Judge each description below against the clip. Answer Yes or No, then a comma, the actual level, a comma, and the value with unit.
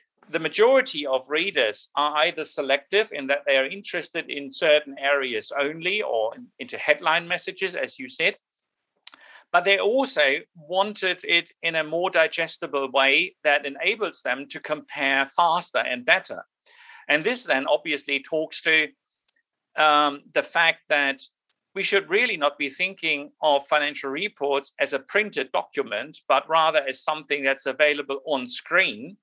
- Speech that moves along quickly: No, average, 150 wpm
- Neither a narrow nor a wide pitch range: Yes, average, 4.9 semitones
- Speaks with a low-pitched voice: No, medium, 155 Hz